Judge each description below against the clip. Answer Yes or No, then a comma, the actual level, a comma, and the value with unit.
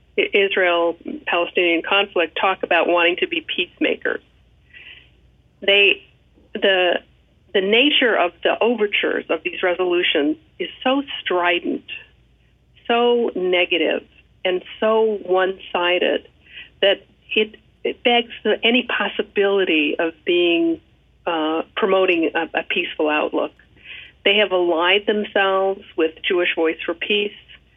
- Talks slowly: Yes, slow, 105 wpm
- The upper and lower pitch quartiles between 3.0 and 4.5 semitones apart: No, average, 5.2 semitones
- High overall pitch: Yes, high, 195 Hz